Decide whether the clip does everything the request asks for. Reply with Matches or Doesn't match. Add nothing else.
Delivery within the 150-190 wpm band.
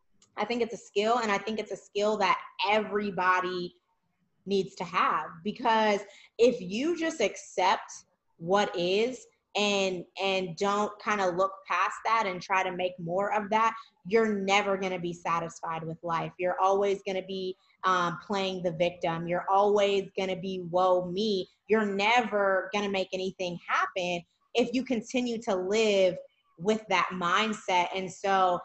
Matches